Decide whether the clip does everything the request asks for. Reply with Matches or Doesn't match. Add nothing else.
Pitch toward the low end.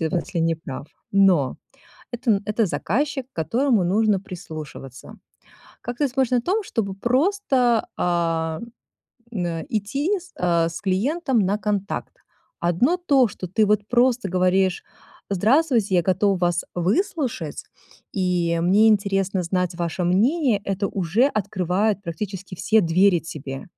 Doesn't match